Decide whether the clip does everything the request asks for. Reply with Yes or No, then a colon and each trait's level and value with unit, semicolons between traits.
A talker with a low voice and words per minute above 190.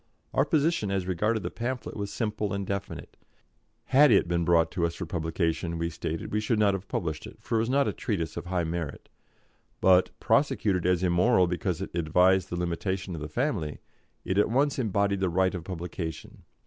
Yes: very low, 95 Hz; average, 200 wpm